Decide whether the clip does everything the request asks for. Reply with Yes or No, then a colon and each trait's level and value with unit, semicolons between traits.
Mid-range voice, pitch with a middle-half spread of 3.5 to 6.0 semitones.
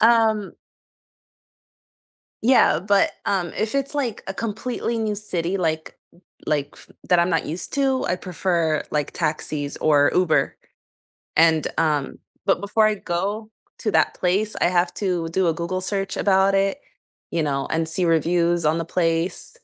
Yes: medium, 180 Hz; average, 3.9 semitones